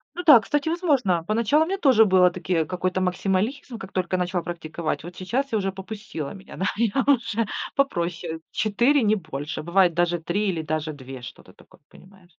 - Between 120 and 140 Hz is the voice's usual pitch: No, high, 190 Hz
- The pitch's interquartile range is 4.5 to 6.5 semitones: Yes, average, 5.1 semitones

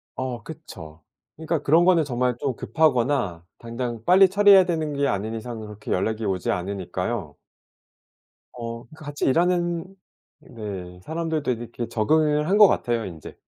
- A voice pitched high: No, low, 125 Hz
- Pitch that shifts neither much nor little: No, wide, 6.7 semitones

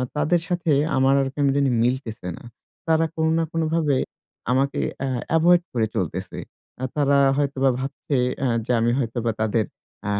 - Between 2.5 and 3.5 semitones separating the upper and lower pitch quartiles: No, average, 4.3 semitones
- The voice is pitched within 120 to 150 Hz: Yes, low, 135 Hz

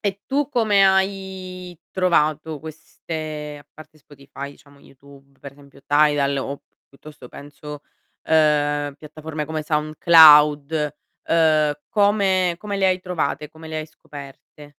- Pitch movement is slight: No, average, 3.6 semitones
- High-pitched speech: No, medium, 155 Hz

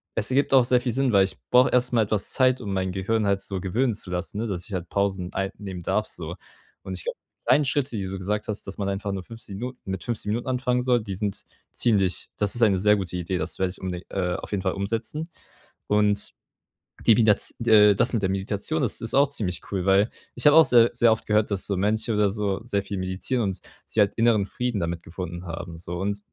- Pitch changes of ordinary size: Yes, average, 3.6 semitones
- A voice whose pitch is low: Yes, low, 100 Hz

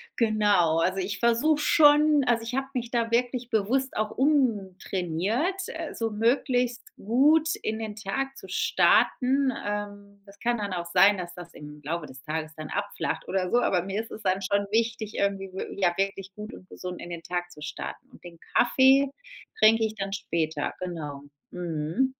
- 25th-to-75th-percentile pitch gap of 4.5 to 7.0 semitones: Yes, average, 5.2 semitones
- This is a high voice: Yes, high, 205 Hz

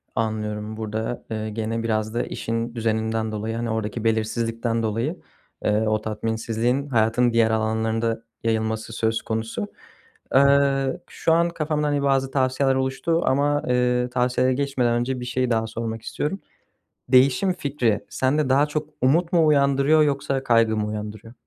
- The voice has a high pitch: No, low, 120 Hz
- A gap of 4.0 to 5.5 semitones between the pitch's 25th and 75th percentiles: No, average, 3.6 semitones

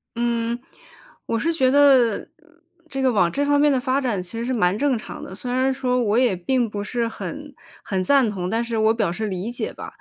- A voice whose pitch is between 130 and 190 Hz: No, high, 235 Hz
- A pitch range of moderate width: Yes, average, 3.8 semitones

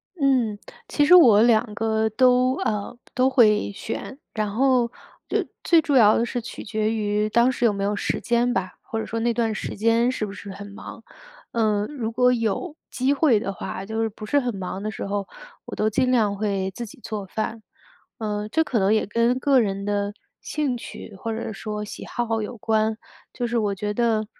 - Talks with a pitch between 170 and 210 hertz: No, high, 220 Hz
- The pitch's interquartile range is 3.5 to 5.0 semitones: No, average, 2.7 semitones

